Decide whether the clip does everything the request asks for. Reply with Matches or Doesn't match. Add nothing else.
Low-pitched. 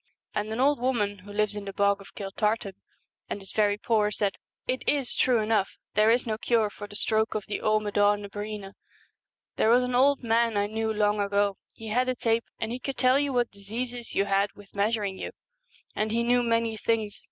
Doesn't match